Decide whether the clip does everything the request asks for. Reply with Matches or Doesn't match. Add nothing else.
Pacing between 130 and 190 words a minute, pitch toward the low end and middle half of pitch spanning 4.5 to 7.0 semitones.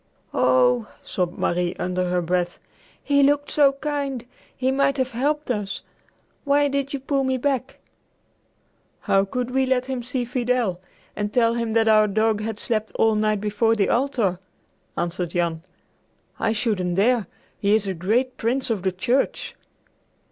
Doesn't match